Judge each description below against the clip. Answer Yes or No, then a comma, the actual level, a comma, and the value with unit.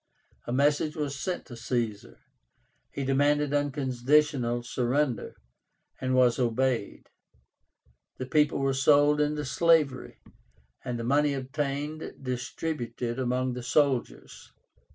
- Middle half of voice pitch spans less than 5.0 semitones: Yes, average, 2.9 semitones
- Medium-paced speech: No, slow, 110 wpm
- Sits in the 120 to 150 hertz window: Yes, low, 135 Hz